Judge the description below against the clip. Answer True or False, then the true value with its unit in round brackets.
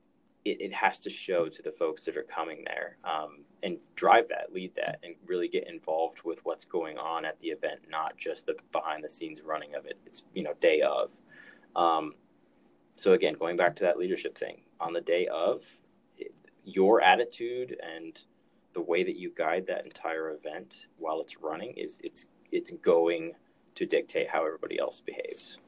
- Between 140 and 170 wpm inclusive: False (190 wpm)